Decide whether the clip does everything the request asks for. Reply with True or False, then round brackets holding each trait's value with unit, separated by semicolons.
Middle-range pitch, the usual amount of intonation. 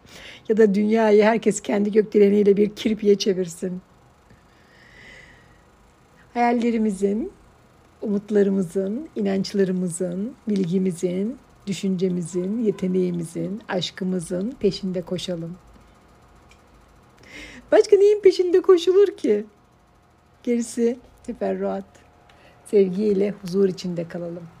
False (200 Hz; 3.0 semitones)